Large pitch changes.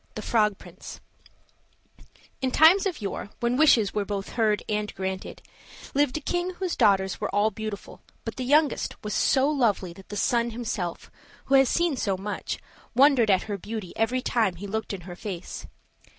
No: average, 4.9 semitones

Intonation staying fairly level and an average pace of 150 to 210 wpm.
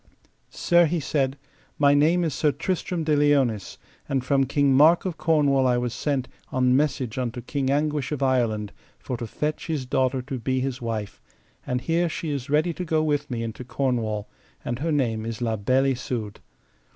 No: average, 3.5 semitones; average, 190 wpm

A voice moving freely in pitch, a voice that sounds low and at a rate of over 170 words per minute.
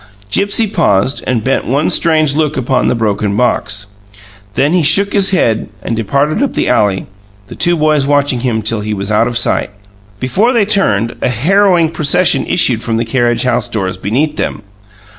Yes: wide, 6.0 semitones; low, 130 Hz; average, 180 wpm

